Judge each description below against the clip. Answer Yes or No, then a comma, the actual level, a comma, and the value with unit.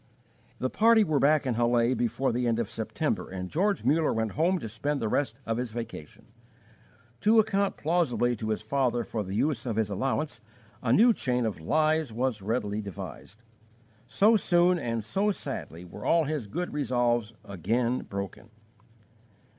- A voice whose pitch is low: Yes, low, 120 Hz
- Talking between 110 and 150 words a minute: No, average, 170 wpm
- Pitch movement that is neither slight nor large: No, wide, 5.8 semitones